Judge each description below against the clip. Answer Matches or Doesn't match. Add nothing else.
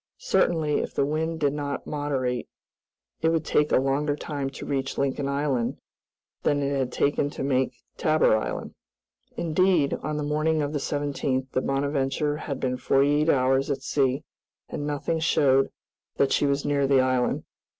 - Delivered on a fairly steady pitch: Matches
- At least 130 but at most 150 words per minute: Doesn't match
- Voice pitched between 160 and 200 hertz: Doesn't match